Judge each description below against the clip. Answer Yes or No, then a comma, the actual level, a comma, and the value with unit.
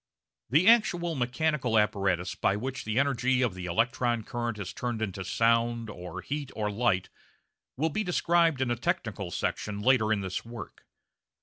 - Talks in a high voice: No, low, 120 Hz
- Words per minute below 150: No, average, 165 wpm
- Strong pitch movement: No, average, 4.2 semitones